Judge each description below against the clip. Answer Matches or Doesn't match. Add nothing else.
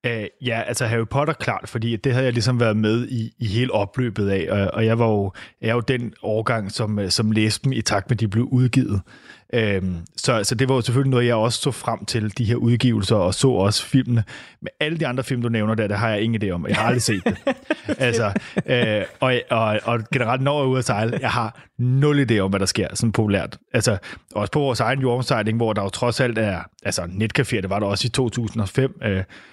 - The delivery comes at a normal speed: Doesn't match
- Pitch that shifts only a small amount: Doesn't match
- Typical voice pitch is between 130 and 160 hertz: Doesn't match